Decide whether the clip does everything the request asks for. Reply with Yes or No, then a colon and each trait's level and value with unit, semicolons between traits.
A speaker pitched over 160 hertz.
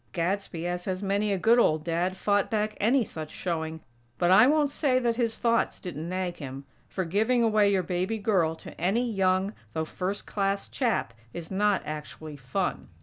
Yes: high, 190 Hz